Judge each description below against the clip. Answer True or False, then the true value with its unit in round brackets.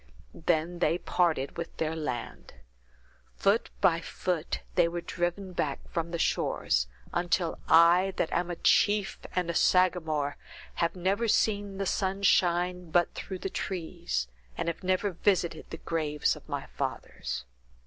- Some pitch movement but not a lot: False (2.2 semitones)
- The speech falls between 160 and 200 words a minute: False (150 wpm)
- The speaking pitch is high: False (175 Hz)